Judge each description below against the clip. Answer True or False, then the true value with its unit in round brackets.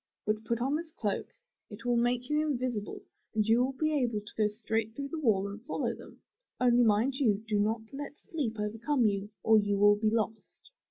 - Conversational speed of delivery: False (210 wpm)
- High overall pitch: True (225 Hz)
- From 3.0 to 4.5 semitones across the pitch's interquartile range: True (3.7 semitones)